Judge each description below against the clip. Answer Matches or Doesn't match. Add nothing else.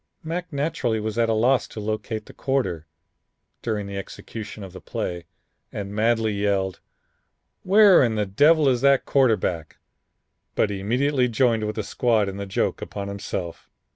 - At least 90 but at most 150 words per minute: Doesn't match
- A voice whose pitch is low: Matches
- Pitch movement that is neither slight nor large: Matches